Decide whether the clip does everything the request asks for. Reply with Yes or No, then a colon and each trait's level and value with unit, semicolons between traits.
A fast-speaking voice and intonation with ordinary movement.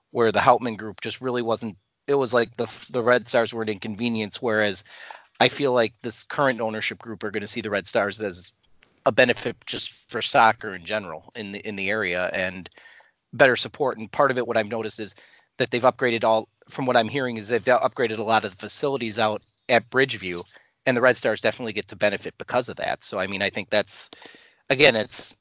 No: fast, 220 wpm; narrow, 2.2 semitones